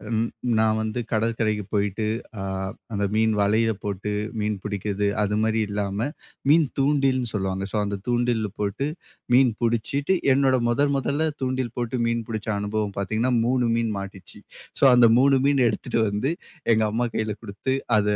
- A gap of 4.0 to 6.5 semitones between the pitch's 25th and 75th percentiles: No, average, 3.4 semitones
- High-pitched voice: No, low, 110 Hz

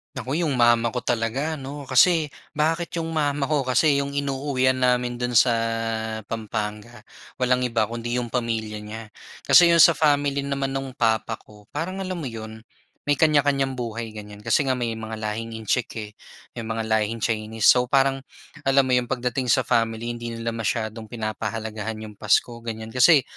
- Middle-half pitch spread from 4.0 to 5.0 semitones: No, average, 3.6 semitones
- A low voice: Yes, low, 120 Hz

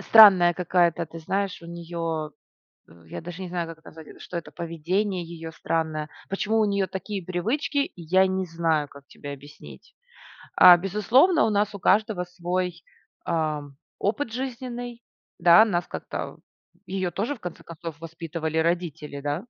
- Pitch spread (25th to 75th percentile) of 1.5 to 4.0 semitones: Yes, average, 3.5 semitones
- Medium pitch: Yes, medium, 175 Hz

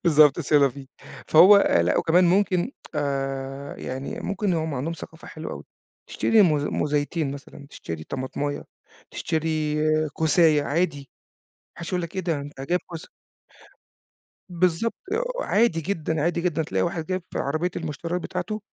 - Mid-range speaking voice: Yes, medium, 160 Hz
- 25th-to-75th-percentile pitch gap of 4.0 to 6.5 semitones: No, average, 3.6 semitones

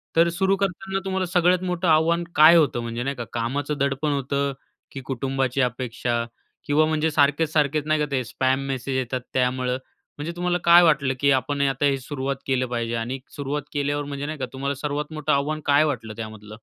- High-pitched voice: No, medium, 140 Hz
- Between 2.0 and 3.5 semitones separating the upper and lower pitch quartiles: Yes, average, 3.1 semitones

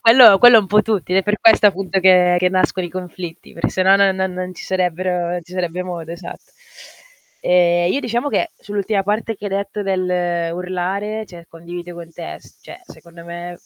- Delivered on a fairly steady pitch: Yes, narrow, 2.3 semitones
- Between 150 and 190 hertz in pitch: Yes, medium, 185 Hz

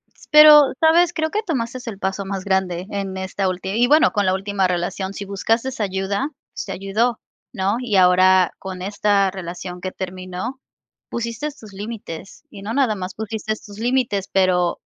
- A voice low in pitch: No, high, 200 Hz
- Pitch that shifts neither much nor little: Yes, average, 3.5 semitones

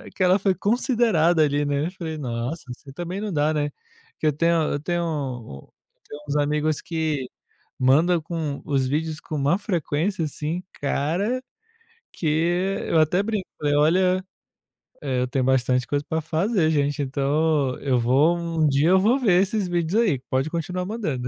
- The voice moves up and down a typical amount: Yes, average, 3.9 semitones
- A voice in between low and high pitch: Yes, medium, 155 Hz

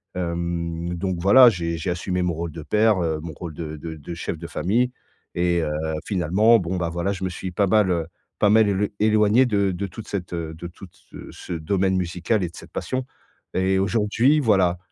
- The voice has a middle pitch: No, very low, 90 Hz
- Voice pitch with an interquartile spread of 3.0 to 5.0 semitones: Yes, average, 3.3 semitones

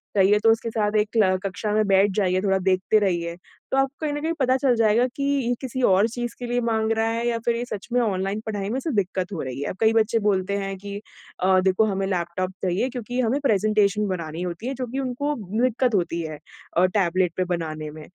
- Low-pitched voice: No, high, 210 Hz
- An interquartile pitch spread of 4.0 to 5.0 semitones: Yes, average, 4.3 semitones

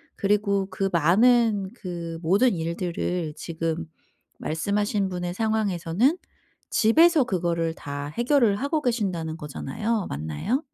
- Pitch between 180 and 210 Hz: Yes, high, 190 Hz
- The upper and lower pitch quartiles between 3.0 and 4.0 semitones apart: No, average, 5.2 semitones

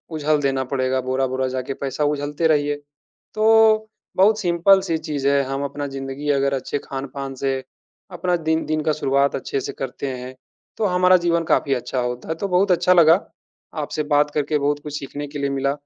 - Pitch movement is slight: No, average, 3.5 semitones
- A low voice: No, medium, 145 Hz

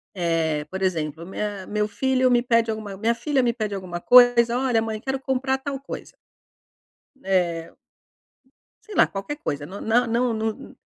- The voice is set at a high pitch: Yes, high, 220 Hz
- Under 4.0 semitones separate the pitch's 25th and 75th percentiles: No, average, 4.7 semitones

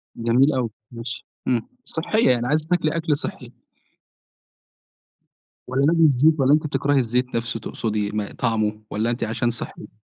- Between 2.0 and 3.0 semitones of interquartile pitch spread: No, average, 4.4 semitones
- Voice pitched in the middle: No, low, 125 Hz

